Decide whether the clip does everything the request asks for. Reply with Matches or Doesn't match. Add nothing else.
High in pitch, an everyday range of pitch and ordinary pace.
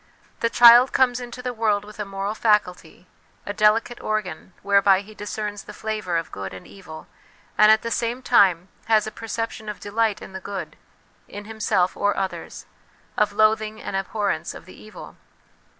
Doesn't match